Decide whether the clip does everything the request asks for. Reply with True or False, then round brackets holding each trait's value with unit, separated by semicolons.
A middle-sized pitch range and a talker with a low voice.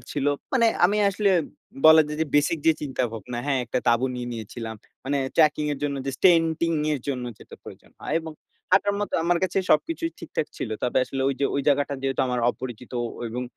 False (4.7 semitones; 145 Hz)